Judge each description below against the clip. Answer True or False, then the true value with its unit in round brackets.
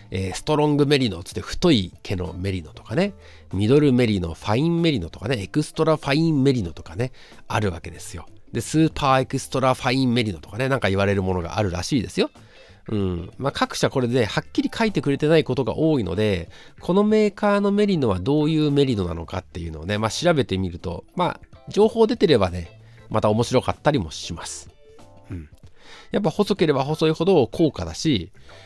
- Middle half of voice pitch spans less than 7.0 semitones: False (8.3 semitones)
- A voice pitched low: True (120 Hz)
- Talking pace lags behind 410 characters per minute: False (425 characters per minute)